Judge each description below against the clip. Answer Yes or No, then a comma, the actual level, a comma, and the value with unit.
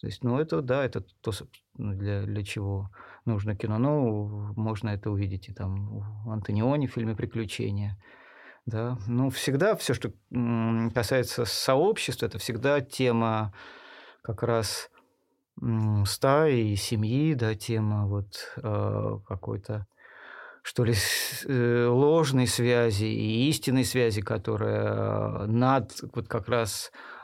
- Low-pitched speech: Yes, low, 115 Hz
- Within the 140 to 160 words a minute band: No, average, 120 wpm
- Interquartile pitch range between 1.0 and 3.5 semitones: Yes, average, 2.9 semitones